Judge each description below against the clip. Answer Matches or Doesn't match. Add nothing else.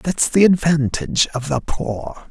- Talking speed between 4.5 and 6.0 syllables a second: Doesn't match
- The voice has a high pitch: Doesn't match